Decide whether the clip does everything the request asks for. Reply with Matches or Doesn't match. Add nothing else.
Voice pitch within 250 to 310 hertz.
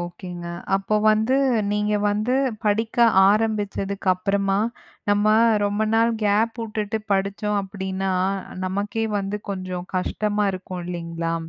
Doesn't match